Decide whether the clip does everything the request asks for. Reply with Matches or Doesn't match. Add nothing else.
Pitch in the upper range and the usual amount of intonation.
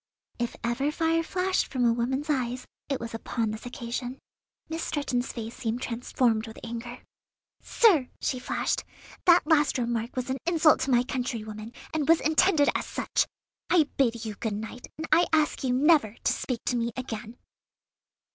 Matches